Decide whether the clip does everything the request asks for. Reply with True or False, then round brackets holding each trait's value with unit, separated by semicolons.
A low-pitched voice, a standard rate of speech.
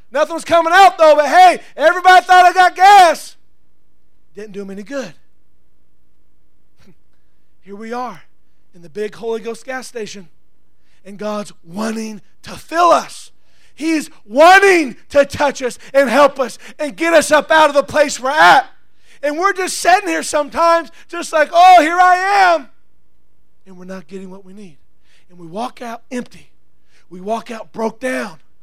False (255 Hz; 170 wpm)